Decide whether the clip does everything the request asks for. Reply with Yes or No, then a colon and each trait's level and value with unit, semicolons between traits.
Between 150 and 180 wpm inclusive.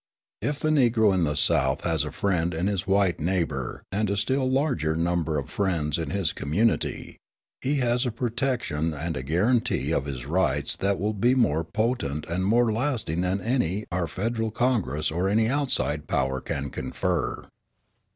Yes: average, 170 wpm